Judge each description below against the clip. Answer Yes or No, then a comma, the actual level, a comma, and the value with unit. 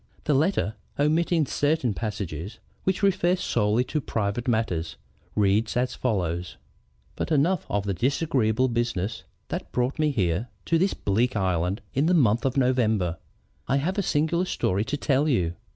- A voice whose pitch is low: Yes, low, 120 Hz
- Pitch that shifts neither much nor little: No, wide, 6.8 semitones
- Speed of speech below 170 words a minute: Yes, average, 155 wpm